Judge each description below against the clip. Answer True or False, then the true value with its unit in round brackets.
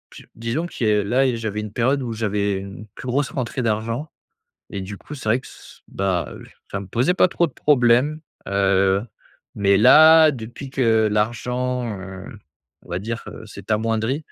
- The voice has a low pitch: True (115 Hz)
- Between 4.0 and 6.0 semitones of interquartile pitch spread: True (4.3 semitones)